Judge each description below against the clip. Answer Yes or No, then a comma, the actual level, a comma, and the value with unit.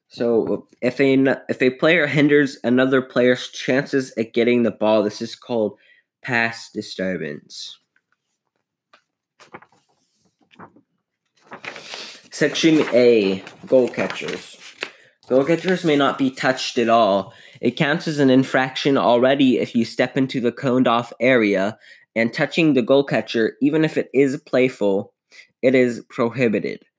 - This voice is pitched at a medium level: No, low, 130 Hz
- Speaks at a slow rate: Yes, slow, 130 wpm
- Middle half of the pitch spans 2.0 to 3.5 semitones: Yes, average, 3.0 semitones